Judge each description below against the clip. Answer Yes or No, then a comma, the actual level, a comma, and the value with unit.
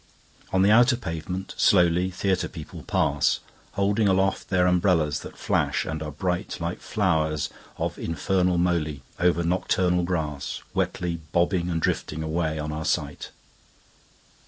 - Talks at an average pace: No, slow, 115 wpm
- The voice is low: Yes, very low, 90 Hz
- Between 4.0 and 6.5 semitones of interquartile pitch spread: No, average, 2.9 semitones